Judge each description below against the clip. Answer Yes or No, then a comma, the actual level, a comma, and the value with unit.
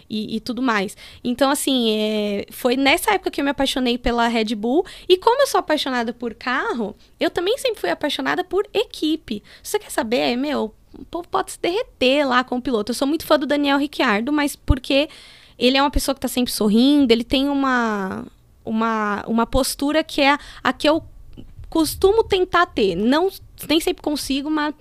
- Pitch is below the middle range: No, very high, 280 Hz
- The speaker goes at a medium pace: No, fast, 200 wpm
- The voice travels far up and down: No, average, 4.8 semitones